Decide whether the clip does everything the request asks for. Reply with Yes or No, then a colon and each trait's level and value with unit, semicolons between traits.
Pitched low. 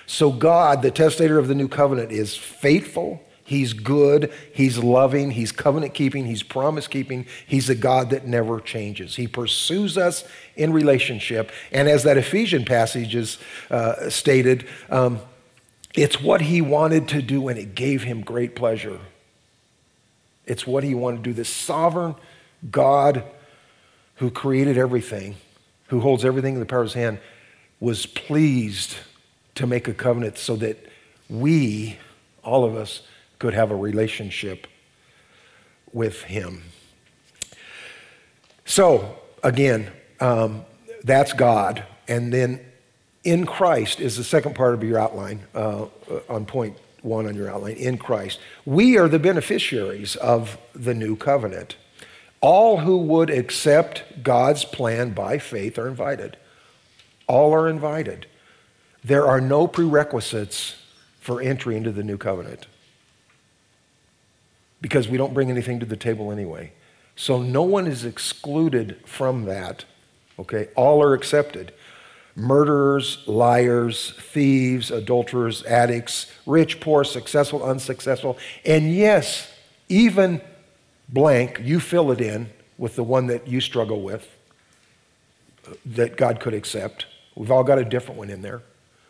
Yes: low, 125 Hz